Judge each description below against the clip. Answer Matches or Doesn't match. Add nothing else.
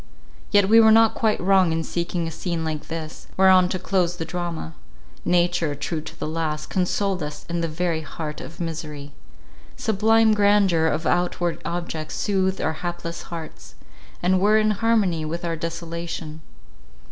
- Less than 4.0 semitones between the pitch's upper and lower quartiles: Matches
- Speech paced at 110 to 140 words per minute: Doesn't match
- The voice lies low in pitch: Doesn't match